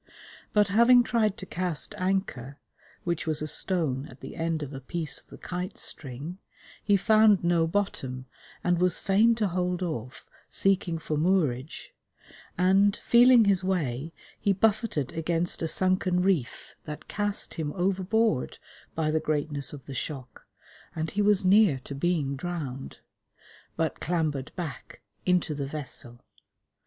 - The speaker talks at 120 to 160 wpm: Yes, average, 145 wpm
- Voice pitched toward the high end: No, medium, 175 Hz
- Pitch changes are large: No, average, 4.7 semitones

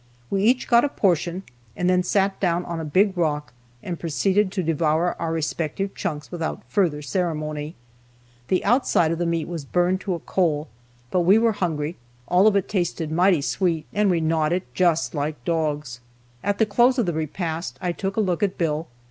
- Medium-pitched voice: Yes, medium, 175 Hz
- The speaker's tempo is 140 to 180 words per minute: No, average, 195 wpm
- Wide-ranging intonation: No, average, 3.4 semitones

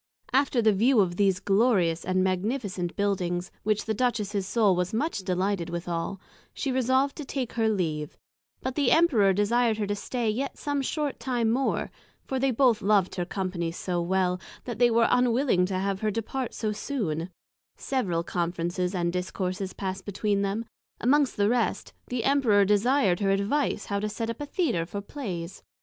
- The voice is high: Yes, high, 205 Hz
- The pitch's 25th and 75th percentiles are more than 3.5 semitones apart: Yes, average, 4.9 semitones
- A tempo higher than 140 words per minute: Yes, average, 175 wpm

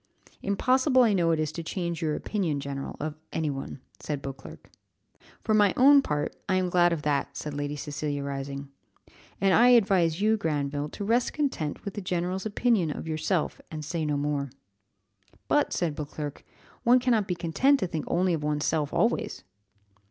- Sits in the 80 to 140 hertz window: No, medium, 165 Hz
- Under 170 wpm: No, average, 180 wpm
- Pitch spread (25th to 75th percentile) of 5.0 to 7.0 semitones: Yes, average, 5.3 semitones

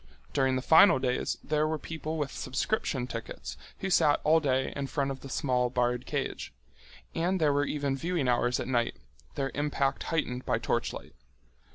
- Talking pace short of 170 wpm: No, average, 175 wpm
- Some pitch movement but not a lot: Yes, average, 3.3 semitones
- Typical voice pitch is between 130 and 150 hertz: Yes, medium, 140 Hz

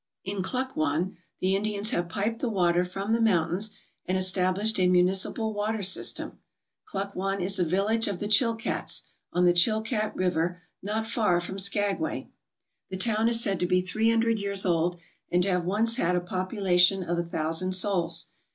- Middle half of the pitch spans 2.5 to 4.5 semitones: Yes, average, 3.2 semitones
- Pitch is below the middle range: No, high, 190 Hz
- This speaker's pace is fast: No, average, 170 wpm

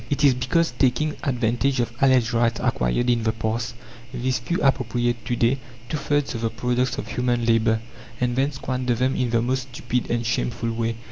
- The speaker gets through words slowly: No, average, 195 wpm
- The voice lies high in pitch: No, low, 120 Hz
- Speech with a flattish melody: Yes, narrow, 2.0 semitones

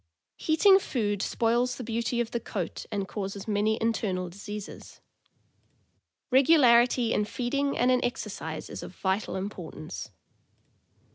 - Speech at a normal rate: No, slow, 130 wpm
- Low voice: No, high, 225 Hz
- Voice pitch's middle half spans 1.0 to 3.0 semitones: No, average, 3.5 semitones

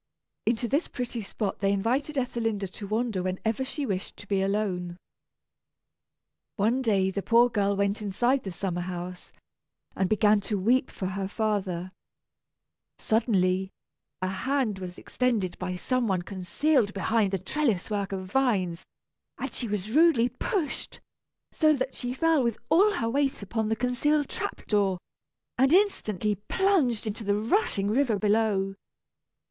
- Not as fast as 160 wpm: Yes, average, 150 wpm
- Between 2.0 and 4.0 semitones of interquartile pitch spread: No, average, 4.6 semitones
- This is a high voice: Yes, high, 215 Hz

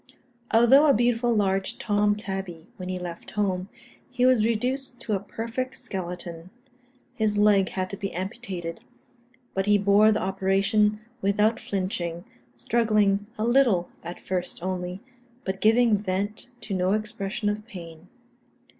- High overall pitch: Yes, high, 205 Hz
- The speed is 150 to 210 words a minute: No, average, 140 wpm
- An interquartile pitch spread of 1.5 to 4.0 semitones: Yes, average, 2.9 semitones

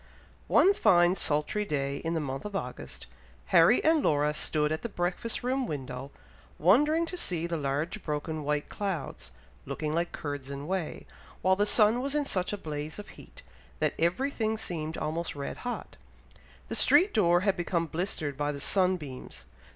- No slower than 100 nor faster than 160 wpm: No, average, 175 wpm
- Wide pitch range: Yes, wide, 5.7 semitones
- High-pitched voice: No, medium, 170 Hz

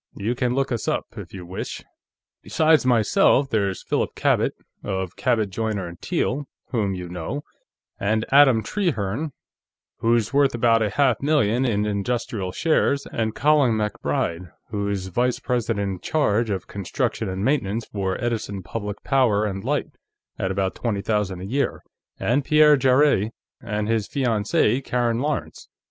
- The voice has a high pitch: No, low, 110 Hz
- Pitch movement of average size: Yes, average, 4.5 semitones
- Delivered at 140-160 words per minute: Yes, average, 155 wpm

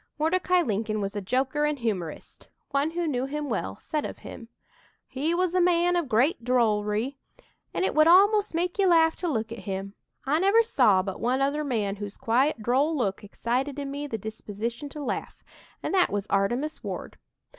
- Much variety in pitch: Yes, wide, 6.8 semitones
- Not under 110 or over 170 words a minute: No, average, 190 wpm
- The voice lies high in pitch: Yes, very high, 270 Hz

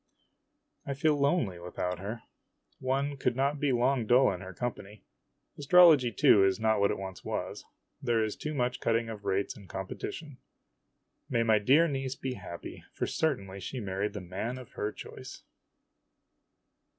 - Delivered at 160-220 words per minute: Yes, average, 165 wpm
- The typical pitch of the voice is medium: No, low, 115 Hz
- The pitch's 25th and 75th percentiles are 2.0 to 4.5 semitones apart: No, wide, 5.5 semitones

